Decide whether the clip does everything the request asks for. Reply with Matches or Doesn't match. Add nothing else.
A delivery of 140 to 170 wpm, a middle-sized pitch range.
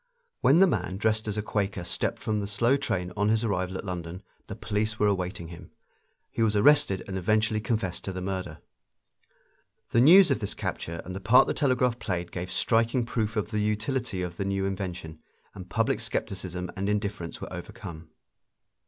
Doesn't match